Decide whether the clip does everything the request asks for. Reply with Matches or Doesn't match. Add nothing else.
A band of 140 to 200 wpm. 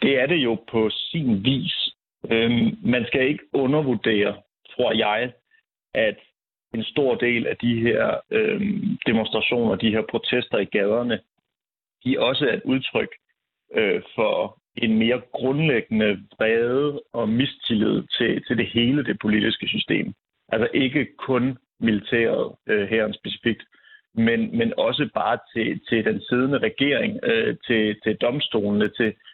Matches